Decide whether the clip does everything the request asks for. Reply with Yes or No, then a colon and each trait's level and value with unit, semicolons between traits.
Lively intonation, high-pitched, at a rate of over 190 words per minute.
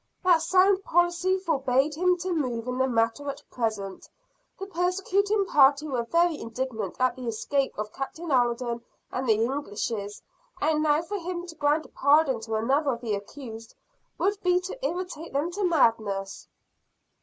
No: wide, 6.8 semitones; very high, 285 Hz; average, 165 wpm